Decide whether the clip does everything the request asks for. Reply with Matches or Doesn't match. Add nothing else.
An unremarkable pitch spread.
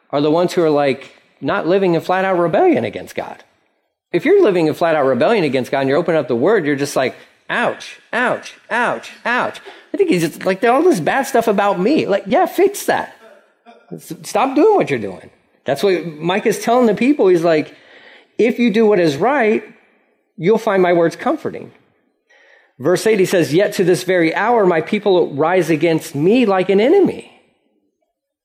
Doesn't match